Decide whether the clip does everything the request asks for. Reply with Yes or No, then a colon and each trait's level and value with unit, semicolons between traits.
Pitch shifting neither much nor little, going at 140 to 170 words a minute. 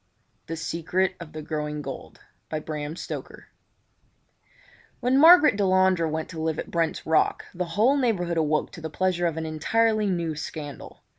Yes: average, 3.3 semitones; average, 145 wpm